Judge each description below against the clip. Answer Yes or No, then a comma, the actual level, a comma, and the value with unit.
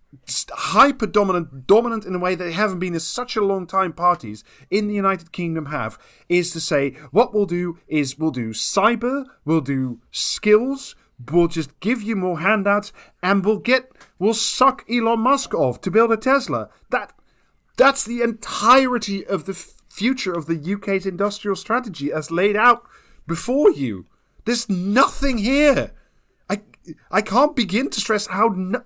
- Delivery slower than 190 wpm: Yes, average, 165 wpm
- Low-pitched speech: No, high, 200 Hz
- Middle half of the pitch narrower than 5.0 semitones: No, average, 5.3 semitones